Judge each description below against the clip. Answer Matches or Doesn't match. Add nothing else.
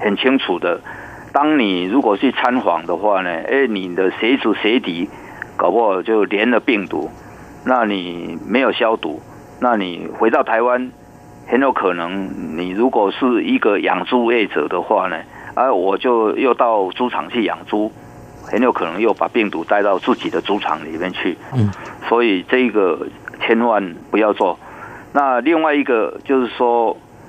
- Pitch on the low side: Matches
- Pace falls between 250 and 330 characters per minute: Doesn't match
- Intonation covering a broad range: Matches